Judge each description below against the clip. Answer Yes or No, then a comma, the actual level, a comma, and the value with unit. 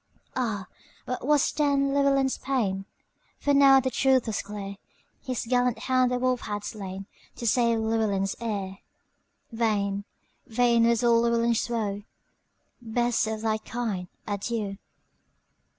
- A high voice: Yes, high, 230 Hz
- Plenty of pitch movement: No, average, 3.4 semitones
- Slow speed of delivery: Yes, slow, 110 wpm